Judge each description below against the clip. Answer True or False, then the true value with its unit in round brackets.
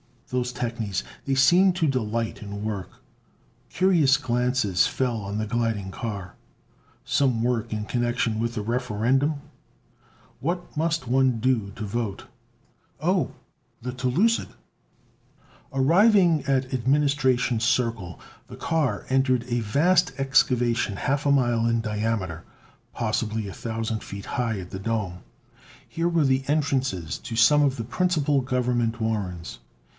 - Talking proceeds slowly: True (130 wpm)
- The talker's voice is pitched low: True (120 Hz)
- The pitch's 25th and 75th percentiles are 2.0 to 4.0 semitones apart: True (3.7 semitones)